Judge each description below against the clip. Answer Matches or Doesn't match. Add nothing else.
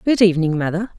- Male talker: Doesn't match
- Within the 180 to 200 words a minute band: Matches